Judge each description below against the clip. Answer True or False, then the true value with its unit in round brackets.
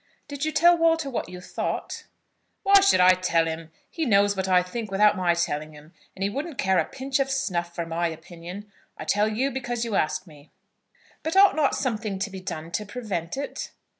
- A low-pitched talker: False (200 Hz)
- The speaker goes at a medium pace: False (210 wpm)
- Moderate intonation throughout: False (7.5 semitones)